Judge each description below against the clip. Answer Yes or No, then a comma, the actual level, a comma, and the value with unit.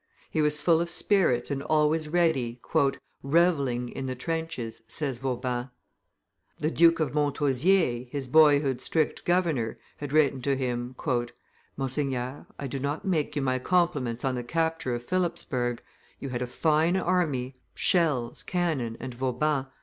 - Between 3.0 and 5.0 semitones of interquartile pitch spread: Yes, average, 4.4 semitones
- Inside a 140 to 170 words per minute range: Yes, average, 145 wpm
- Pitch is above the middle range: No, medium, 140 Hz